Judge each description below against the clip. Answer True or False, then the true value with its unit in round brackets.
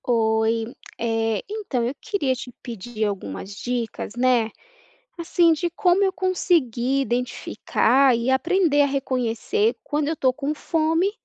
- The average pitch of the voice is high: True (265 Hz)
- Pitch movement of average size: False (6.2 semitones)